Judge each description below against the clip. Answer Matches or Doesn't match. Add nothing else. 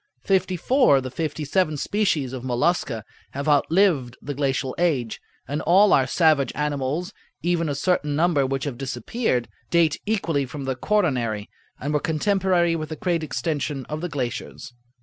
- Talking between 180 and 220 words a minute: Doesn't match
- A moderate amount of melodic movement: Matches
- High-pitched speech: Doesn't match